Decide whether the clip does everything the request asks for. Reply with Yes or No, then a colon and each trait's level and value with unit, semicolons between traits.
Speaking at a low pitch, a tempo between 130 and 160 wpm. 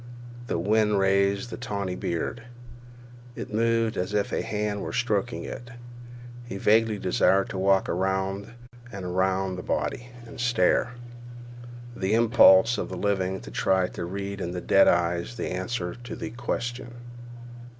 Yes: low, 100 Hz; average, 150 wpm